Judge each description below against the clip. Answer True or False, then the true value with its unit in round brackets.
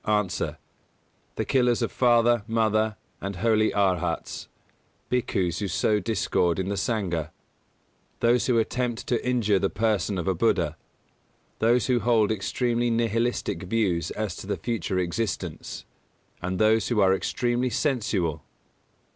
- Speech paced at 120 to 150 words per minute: True (140 wpm)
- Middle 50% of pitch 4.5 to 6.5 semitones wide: False (3.7 semitones)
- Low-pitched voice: True (110 Hz)